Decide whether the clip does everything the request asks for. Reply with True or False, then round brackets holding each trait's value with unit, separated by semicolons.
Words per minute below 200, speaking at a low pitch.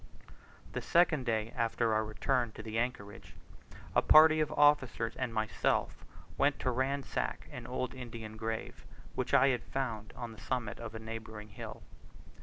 True (160 wpm; 115 Hz)